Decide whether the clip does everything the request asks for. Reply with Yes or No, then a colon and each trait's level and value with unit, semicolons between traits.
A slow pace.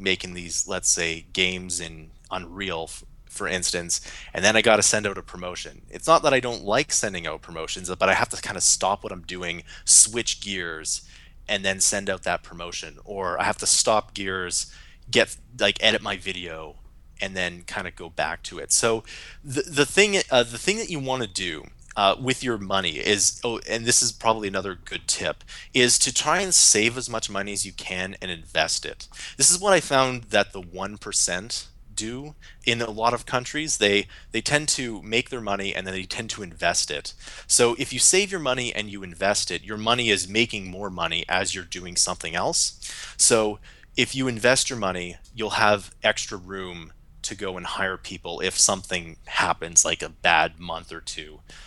No: fast, 205 wpm